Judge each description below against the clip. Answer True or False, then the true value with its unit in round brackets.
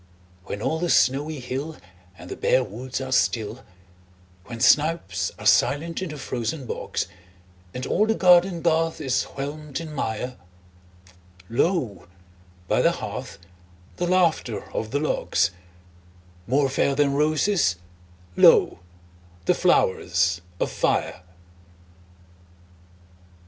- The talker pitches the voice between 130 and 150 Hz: True (140 Hz)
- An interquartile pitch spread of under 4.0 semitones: False (5.3 semitones)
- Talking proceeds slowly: True (120 wpm)